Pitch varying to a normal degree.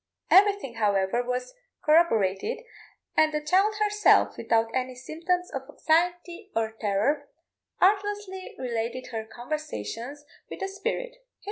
No: wide, 8.2 semitones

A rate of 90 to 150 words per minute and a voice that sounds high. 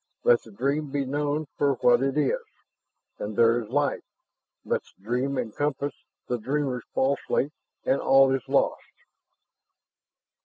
No: average, 140 wpm; low, 135 Hz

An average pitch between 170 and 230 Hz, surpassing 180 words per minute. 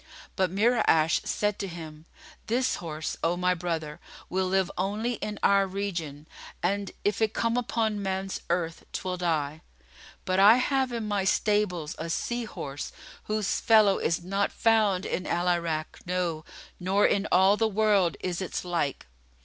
No: high, 190 Hz; average, 155 wpm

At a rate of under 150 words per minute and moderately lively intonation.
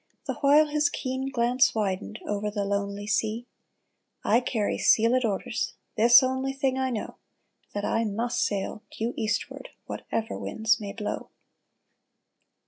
Yes: average, 140 wpm; average, 3.7 semitones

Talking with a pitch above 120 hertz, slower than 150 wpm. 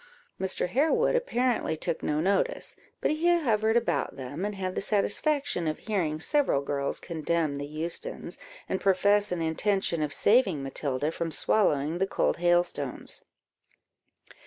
Yes: medium, 185 Hz; average, 140 wpm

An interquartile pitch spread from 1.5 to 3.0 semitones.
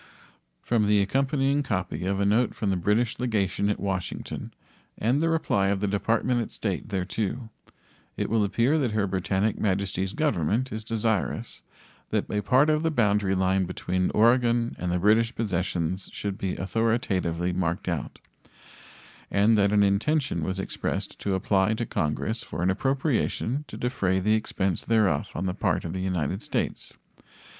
No: average, 3.6 semitones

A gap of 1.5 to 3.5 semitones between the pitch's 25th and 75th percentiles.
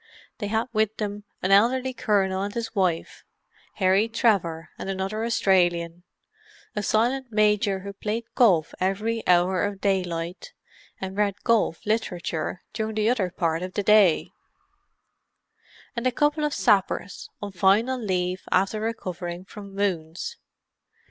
Yes: average, 3.1 semitones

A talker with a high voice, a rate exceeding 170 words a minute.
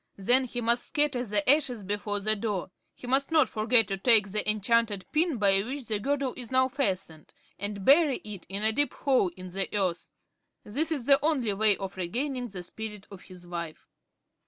Yes: high, 220 Hz; average, 195 wpm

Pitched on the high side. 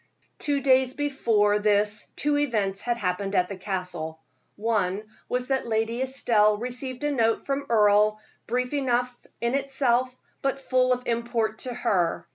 Yes: high, 235 Hz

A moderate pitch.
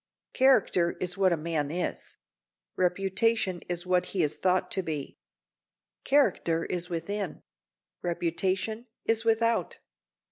Yes: medium, 180 Hz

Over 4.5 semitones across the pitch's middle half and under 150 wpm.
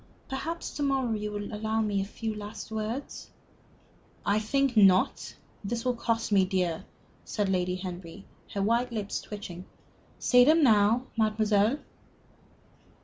No: average, 3.0 semitones; average, 140 wpm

